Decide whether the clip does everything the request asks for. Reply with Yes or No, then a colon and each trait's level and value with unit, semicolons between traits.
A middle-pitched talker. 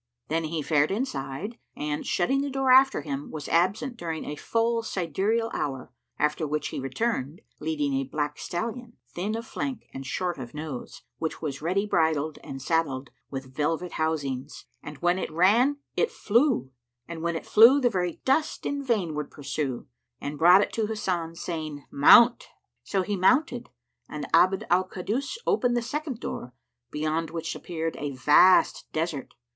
Yes: medium, 165 Hz